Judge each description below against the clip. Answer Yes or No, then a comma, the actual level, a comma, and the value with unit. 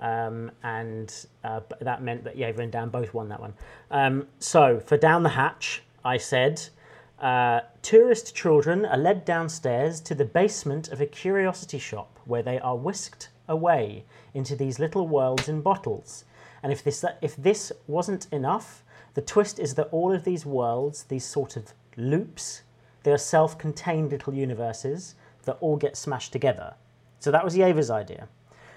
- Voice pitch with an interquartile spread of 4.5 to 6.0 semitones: Yes, average, 4.8 semitones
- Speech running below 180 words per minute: Yes, average, 165 wpm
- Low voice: No, medium, 145 Hz